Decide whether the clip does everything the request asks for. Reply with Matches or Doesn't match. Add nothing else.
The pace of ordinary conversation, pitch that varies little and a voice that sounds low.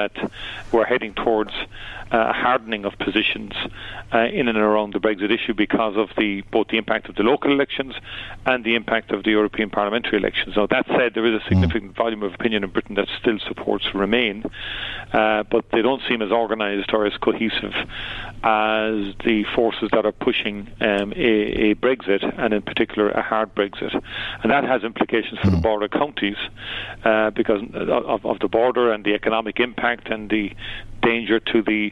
Matches